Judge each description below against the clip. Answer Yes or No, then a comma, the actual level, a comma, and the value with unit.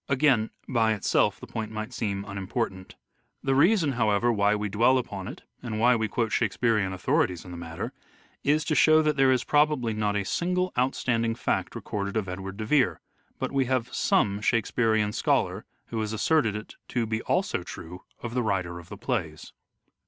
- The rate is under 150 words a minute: No, average, 185 wpm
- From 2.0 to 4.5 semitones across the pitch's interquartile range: Yes, average, 4.1 semitones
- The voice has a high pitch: No, low, 110 Hz